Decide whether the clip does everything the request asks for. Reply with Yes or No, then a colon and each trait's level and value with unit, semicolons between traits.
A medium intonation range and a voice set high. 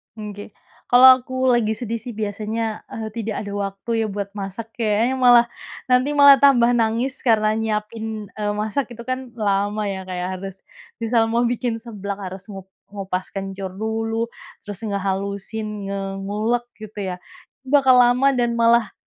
Yes: average, 3.0 semitones; high, 220 Hz